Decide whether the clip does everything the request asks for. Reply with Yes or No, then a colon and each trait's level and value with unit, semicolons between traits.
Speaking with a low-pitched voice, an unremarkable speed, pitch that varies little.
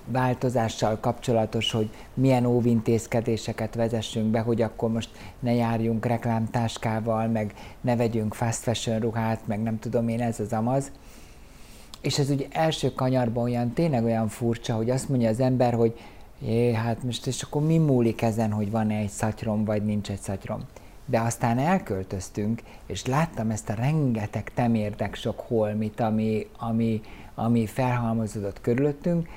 Yes: low, 115 Hz; average, 145 wpm; narrow, 2.0 semitones